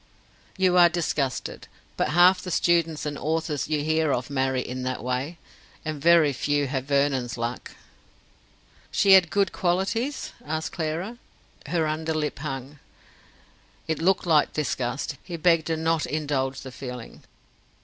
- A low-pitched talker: No, medium, 155 Hz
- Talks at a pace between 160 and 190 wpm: No, average, 145 wpm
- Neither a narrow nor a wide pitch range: Yes, average, 3.9 semitones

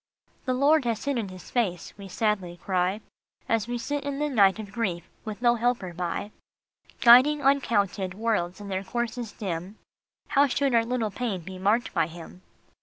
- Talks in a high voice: Yes, high, 215 Hz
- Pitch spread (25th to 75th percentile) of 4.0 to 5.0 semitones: Yes, average, 4.6 semitones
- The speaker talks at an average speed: Yes, average, 180 wpm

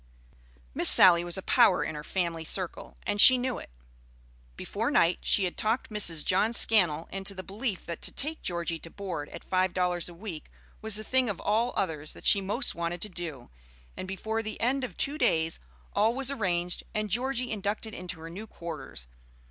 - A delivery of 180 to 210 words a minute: Yes, average, 195 wpm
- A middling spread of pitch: Yes, average, 4.3 semitones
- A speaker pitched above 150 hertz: Yes, high, 190 Hz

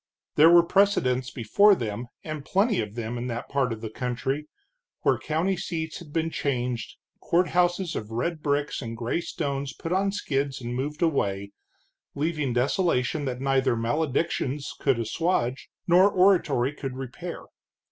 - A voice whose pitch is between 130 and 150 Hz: Yes, medium, 140 Hz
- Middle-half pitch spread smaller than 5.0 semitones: No, average, 5.3 semitones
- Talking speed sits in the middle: Yes, average, 150 wpm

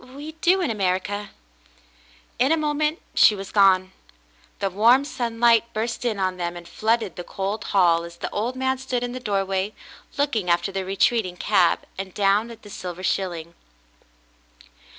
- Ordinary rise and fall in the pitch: Yes, average, 4.4 semitones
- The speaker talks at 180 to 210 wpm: No, average, 165 wpm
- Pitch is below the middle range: No, high, 205 Hz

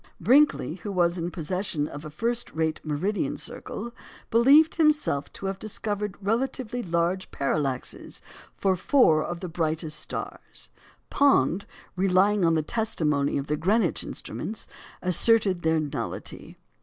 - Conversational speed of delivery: No, slow, 130 wpm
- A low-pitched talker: No, medium, 185 Hz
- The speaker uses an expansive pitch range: Yes, wide, 5.8 semitones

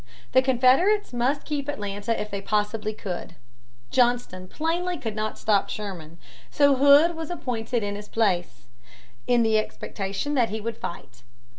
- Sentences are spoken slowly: No, average, 150 wpm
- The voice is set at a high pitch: Yes, high, 225 Hz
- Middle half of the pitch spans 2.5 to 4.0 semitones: No, wide, 5.5 semitones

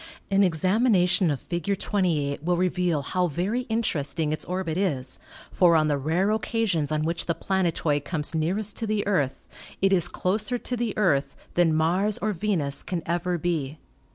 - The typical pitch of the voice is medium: Yes, medium, 175 Hz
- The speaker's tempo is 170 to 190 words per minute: Yes, average, 175 wpm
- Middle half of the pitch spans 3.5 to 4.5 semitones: Yes, average, 4.1 semitones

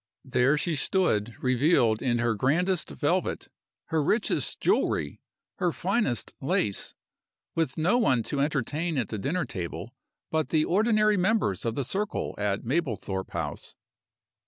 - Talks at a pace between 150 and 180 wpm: No, slow, 135 wpm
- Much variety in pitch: Yes, wide, 7.6 semitones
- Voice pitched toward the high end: No, medium, 140 Hz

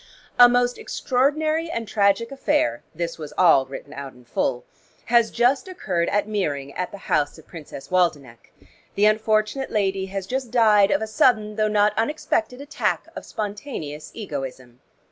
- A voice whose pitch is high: Yes, high, 205 Hz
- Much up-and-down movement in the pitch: Yes, wide, 7.2 semitones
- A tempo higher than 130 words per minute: Yes, average, 160 wpm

